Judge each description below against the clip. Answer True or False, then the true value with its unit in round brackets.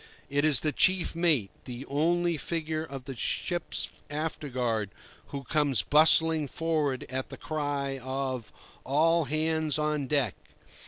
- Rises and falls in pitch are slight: False (3.1 semitones)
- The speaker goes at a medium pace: False (130 wpm)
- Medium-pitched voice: True (150 Hz)